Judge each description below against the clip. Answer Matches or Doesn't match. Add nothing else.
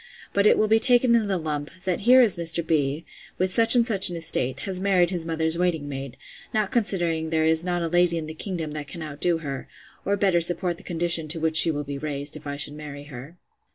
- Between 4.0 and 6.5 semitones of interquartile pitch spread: Doesn't match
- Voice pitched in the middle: Matches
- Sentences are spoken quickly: Matches